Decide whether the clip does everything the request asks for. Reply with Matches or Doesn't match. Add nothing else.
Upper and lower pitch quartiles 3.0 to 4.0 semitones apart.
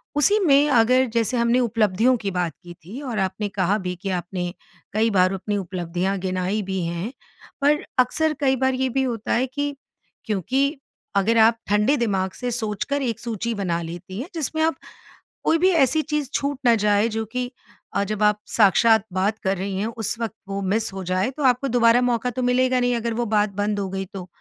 Doesn't match